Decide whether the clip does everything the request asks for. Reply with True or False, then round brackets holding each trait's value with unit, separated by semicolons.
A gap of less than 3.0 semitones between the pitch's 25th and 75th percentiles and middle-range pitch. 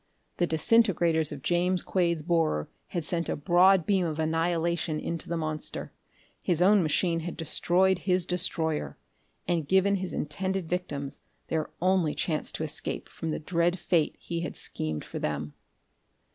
True (2.4 semitones; 170 Hz)